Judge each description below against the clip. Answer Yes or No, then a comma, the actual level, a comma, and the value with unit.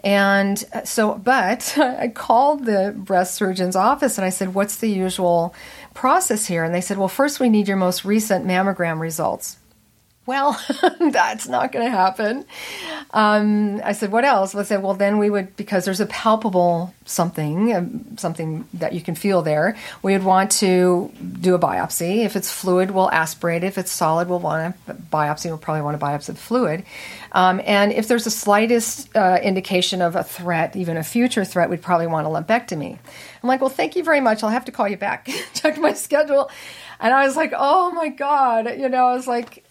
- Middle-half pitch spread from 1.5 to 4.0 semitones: No, average, 4.8 semitones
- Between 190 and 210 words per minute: Yes, average, 200 wpm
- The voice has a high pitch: Yes, high, 200 Hz